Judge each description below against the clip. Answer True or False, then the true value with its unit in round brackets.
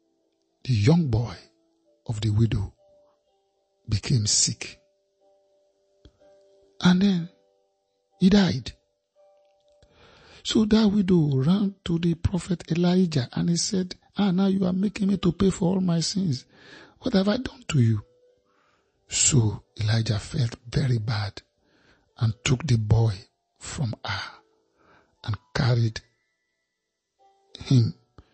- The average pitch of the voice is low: False (170 Hz)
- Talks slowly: True (115 wpm)